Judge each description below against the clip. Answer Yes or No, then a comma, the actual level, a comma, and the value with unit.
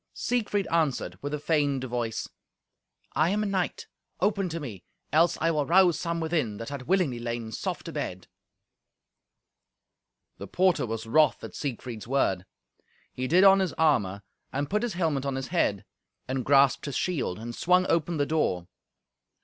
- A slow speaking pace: No, average, 165 wpm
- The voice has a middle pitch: Yes, medium, 145 Hz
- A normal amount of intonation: No, wide, 6.1 semitones